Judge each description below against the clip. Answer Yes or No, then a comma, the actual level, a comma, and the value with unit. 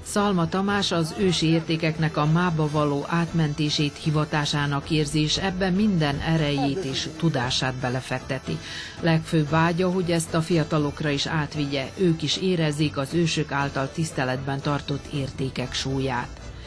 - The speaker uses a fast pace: No, average, 125 wpm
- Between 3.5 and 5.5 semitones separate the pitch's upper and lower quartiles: No, average, 2.9 semitones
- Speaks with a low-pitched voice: No, medium, 155 Hz